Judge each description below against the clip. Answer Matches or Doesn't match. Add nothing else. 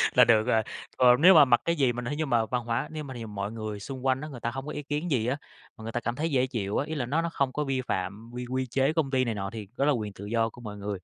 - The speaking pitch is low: Matches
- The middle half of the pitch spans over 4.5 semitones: Doesn't match